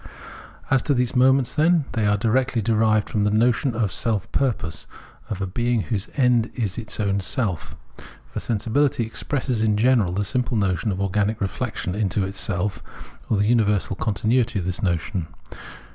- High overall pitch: No, low, 110 Hz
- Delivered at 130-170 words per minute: Yes, average, 165 wpm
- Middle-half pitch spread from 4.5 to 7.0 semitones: No, average, 3.5 semitones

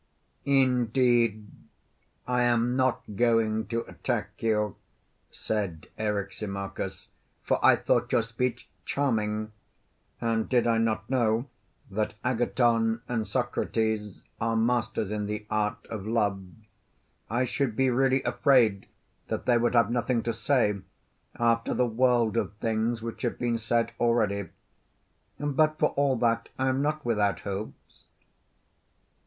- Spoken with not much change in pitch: Yes, narrow, 2.3 semitones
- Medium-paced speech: No, slow, 130 wpm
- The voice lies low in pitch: Yes, low, 115 Hz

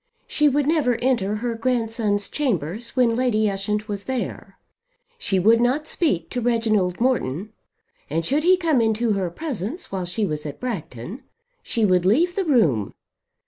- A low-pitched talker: No, high, 225 Hz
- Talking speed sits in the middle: Yes, average, 160 wpm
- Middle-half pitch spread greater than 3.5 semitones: Yes, average, 4.9 semitones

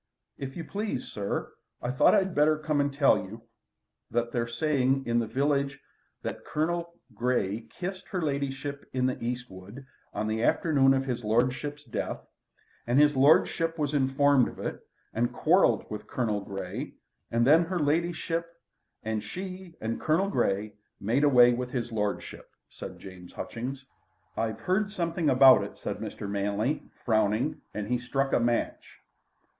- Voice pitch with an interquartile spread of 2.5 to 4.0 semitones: No, average, 4.7 semitones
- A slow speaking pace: No, average, 160 wpm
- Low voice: Yes, low, 130 Hz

